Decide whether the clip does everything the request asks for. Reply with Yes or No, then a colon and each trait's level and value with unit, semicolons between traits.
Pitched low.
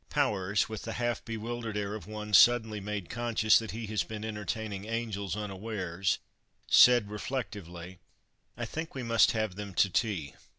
Yes: low, 105 Hz